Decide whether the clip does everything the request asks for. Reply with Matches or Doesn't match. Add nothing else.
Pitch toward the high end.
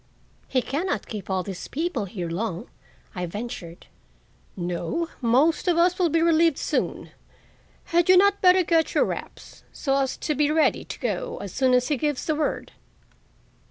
Matches